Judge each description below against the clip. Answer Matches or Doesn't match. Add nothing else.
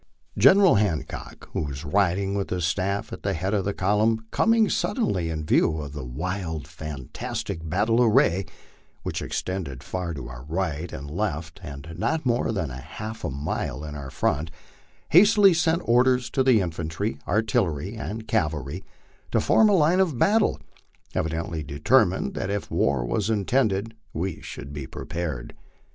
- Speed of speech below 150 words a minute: Doesn't match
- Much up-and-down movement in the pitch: Matches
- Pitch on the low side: Matches